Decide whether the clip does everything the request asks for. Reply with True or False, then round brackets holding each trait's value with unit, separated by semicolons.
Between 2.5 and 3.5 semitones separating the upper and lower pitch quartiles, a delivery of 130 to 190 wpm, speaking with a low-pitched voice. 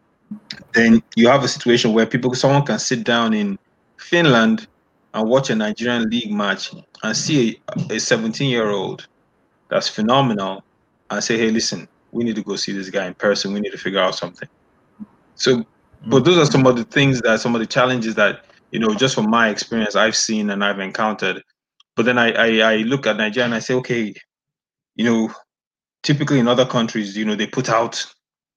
False (2.8 semitones; 200 wpm; 115 Hz)